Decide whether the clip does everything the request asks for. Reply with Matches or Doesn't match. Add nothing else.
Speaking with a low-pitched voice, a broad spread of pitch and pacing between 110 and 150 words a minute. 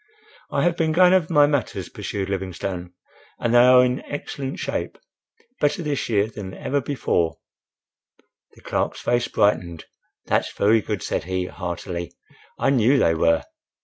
Matches